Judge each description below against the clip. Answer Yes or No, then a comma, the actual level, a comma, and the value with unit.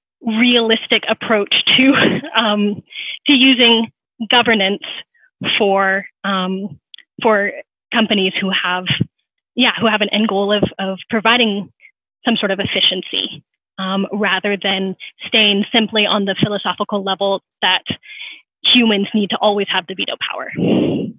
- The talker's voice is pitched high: Yes, high, 210 Hz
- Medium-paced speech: No, slow, 125 wpm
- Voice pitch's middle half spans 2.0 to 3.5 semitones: Yes, average, 2.7 semitones